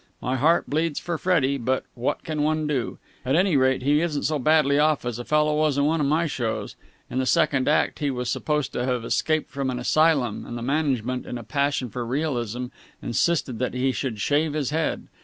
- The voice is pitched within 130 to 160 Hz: Yes, medium, 140 Hz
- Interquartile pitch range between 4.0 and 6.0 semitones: No, average, 3.4 semitones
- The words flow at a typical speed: No, fast, 215 wpm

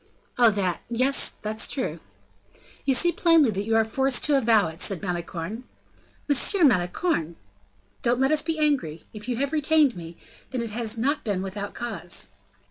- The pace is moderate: Yes, average, 170 wpm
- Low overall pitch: No, high, 235 Hz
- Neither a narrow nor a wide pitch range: No, wide, 5.9 semitones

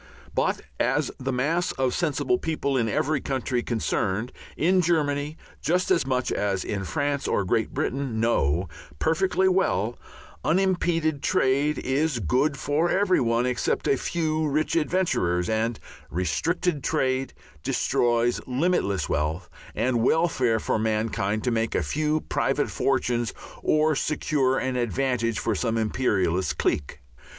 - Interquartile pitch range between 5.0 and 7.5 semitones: Yes, wide, 5.6 semitones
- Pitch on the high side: No, low, 130 Hz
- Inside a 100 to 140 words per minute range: Yes, slow, 135 wpm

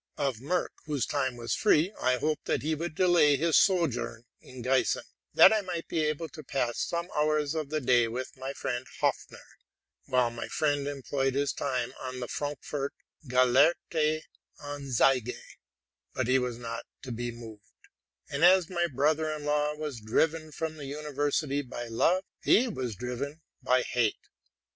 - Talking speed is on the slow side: No, average, 165 wpm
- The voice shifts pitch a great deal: No, average, 3.6 semitones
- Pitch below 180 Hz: Yes, medium, 140 Hz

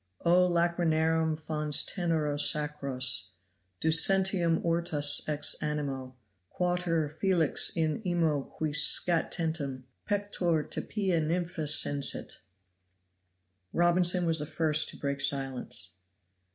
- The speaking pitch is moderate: Yes, medium, 160 Hz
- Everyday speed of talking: No, slow, 100 wpm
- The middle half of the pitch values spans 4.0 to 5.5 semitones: No, average, 2.7 semitones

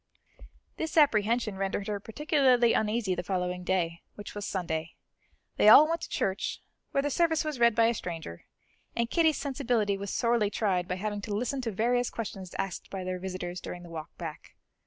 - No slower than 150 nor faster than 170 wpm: No, average, 185 wpm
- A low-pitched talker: No, high, 210 Hz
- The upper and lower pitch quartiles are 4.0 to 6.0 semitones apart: Yes, average, 4.9 semitones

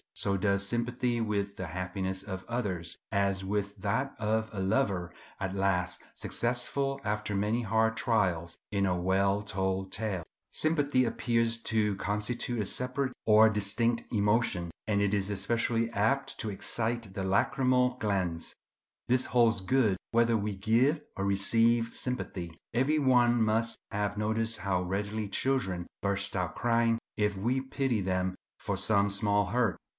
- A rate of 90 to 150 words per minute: Yes, average, 145 wpm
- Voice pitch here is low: Yes, low, 105 Hz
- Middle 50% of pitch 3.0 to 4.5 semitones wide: Yes, average, 3.3 semitones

